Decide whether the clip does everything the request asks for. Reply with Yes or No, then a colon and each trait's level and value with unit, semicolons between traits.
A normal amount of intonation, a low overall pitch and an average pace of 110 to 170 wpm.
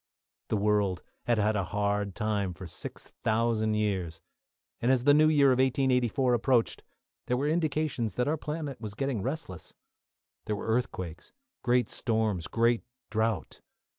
Yes: average, 4.2 semitones; low, 115 Hz; average, 150 wpm